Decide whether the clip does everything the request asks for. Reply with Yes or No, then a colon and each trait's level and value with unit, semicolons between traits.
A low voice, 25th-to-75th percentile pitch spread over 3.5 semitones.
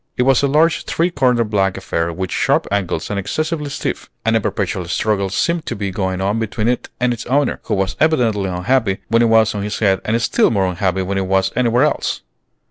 Yes: low, 105 Hz; average, 4.5 semitones